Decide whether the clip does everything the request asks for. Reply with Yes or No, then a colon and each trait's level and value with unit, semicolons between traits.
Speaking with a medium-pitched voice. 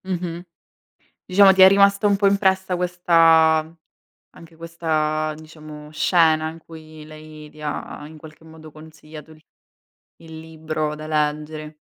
Yes: medium, 160 Hz